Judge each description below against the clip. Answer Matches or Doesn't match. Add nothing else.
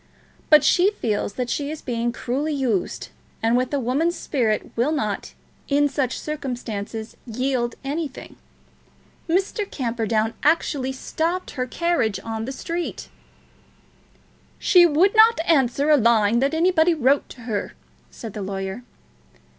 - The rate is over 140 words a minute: Doesn't match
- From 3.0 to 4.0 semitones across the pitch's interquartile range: Doesn't match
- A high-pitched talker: Matches